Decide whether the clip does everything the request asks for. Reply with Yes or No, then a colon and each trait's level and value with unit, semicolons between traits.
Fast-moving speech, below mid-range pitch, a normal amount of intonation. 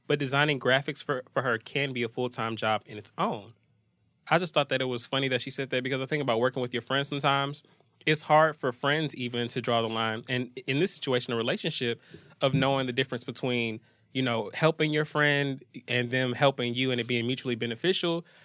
Yes: fast, 220 wpm; low, 130 Hz; average, 3.1 semitones